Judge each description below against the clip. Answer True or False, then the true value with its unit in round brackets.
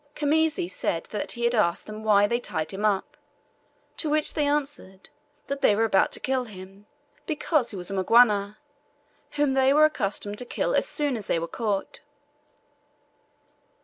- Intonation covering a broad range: True (6.2 semitones)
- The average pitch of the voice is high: True (220 Hz)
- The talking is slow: False (170 wpm)